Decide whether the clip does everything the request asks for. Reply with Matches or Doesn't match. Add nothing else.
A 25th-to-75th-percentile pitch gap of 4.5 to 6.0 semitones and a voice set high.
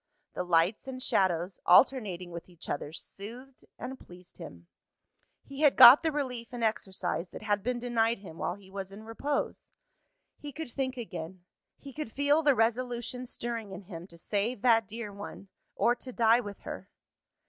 Matches